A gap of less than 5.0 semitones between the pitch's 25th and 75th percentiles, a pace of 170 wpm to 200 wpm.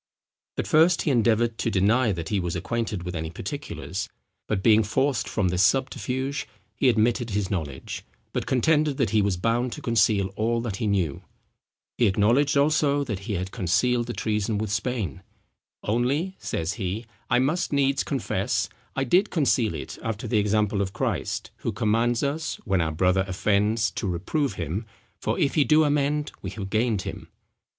No: average, 5.3 semitones; average, 175 wpm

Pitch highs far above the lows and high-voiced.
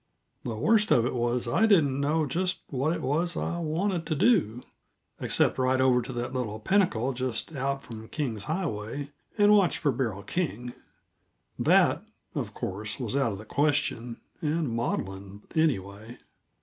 No: wide, 5.7 semitones; low, 130 Hz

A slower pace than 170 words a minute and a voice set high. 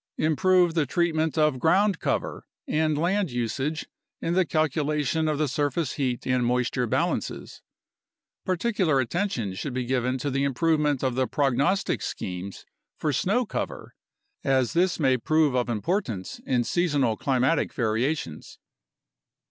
No: average, 140 wpm; medium, 145 Hz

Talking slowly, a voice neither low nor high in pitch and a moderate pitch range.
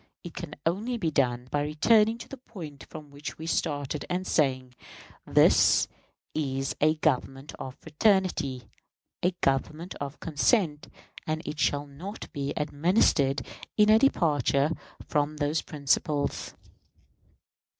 Yes: slow, 130 wpm; medium, 150 Hz; average, 3.6 semitones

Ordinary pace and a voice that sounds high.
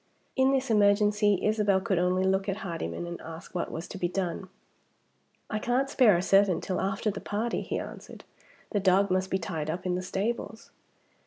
Yes: average, 190 wpm; high, 195 Hz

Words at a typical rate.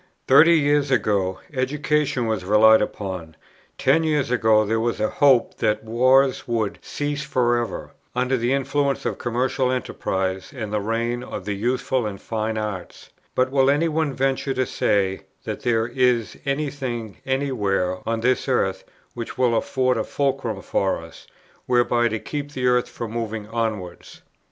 Yes: average, 165 wpm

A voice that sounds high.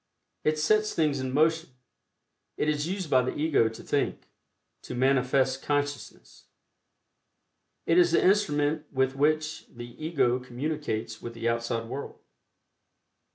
No: medium, 145 Hz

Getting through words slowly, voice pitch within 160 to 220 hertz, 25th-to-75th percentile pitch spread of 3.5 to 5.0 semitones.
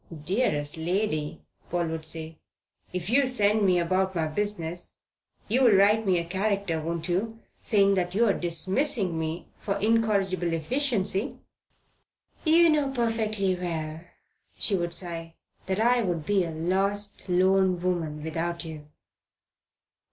Yes: slow, 130 wpm; medium, 185 Hz; average, 3.9 semitones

